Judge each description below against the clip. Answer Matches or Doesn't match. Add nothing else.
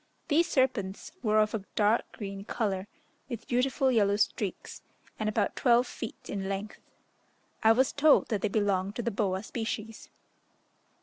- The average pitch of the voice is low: Doesn't match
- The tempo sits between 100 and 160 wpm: Matches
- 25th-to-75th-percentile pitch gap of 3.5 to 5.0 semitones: Doesn't match